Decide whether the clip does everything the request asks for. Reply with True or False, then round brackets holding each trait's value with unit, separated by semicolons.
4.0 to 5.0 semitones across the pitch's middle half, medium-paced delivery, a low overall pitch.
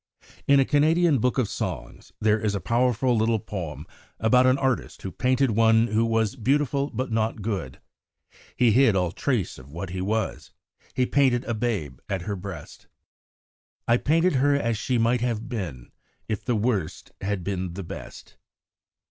True (4.5 semitones; 165 wpm; 115 Hz)